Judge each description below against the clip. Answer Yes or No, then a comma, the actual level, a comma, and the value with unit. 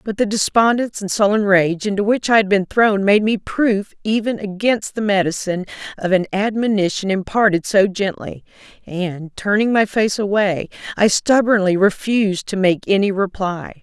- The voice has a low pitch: No, high, 200 Hz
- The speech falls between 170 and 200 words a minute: No, average, 160 wpm